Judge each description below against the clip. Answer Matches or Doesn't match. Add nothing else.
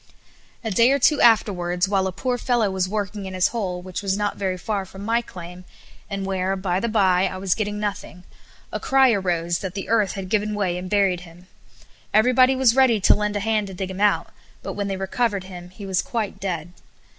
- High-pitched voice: Matches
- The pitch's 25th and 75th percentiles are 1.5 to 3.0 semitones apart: Matches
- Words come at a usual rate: Doesn't match